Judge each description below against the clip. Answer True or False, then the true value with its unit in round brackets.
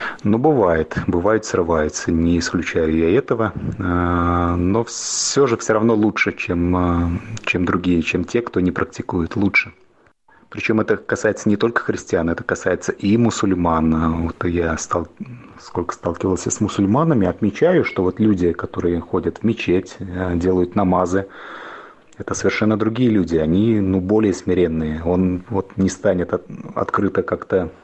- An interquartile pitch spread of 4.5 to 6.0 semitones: False (3.3 semitones)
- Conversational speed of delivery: True (140 wpm)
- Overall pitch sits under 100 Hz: True (90 Hz)